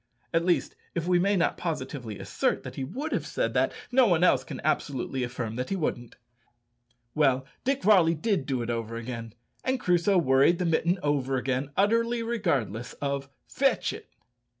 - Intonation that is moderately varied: No, wide, 6.3 semitones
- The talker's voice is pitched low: No, medium, 150 Hz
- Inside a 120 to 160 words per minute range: No, average, 175 wpm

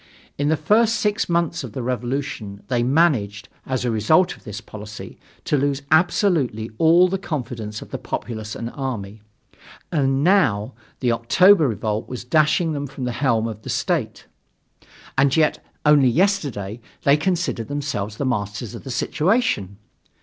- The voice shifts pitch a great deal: Yes, wide, 6.1 semitones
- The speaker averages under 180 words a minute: Yes, average, 155 wpm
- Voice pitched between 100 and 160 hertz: Yes, low, 135 Hz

